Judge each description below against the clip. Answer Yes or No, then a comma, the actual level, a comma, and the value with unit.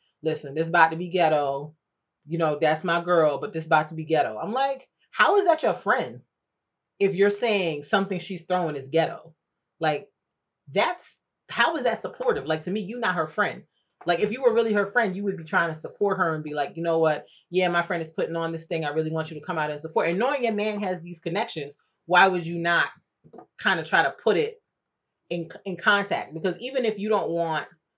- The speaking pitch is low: No, medium, 170 Hz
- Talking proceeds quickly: Yes, fast, 235 wpm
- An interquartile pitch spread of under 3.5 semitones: No, average, 4.3 semitones